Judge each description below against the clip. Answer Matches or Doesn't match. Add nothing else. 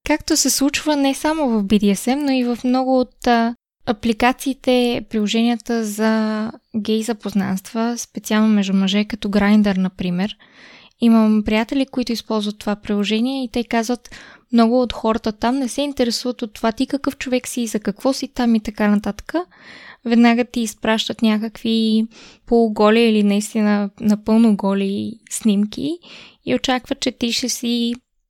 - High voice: Matches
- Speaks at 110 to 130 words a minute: Doesn't match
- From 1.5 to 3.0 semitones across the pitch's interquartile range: Matches